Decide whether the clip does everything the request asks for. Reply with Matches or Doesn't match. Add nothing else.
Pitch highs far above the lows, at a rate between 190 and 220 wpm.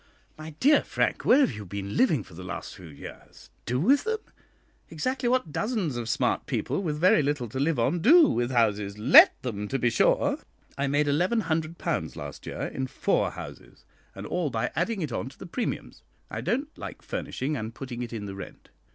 Matches